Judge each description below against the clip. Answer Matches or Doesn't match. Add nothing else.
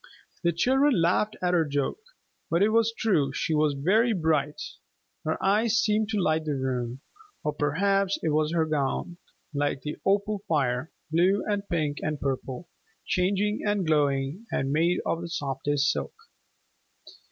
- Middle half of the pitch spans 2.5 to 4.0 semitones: Doesn't match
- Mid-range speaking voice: Matches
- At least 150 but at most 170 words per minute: Matches